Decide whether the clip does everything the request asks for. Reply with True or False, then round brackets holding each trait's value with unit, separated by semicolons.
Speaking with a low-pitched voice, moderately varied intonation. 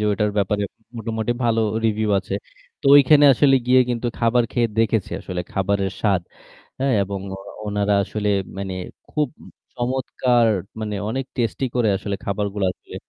True (110 Hz; 3.2 semitones)